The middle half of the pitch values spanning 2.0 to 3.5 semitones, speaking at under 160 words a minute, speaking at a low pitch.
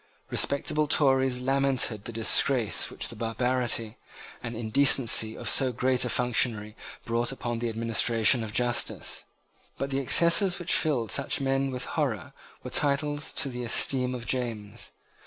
Yes: average, 3.0 semitones; average, 145 wpm; low, 125 Hz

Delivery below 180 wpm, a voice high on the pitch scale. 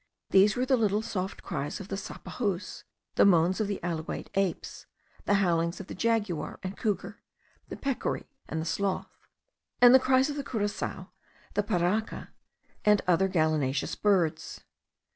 Yes: average, 155 wpm; high, 195 Hz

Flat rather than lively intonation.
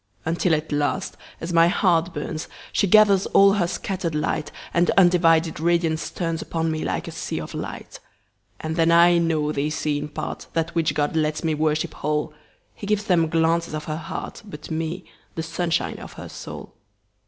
Yes: narrow, 1.9 semitones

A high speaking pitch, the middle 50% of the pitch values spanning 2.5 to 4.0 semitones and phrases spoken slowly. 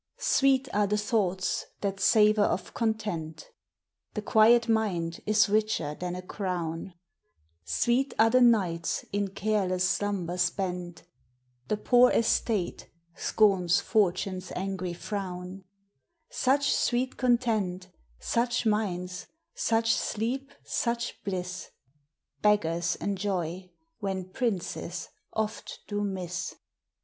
Yes: high, 200 Hz; average, 3.5 semitones; slow, 105 wpm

